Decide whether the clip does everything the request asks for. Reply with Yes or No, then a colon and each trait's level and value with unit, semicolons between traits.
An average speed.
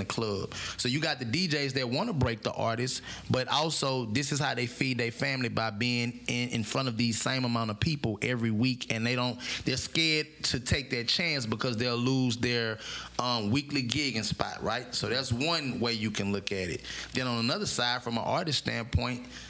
No: fast, 220 wpm